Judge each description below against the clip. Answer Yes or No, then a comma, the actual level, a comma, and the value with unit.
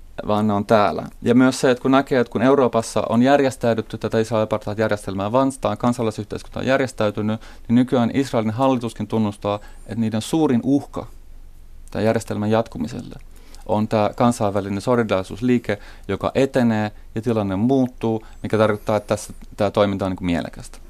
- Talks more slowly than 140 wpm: No, average, 150 wpm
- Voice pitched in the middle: No, low, 110 Hz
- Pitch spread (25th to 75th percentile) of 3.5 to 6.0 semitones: No, average, 2.7 semitones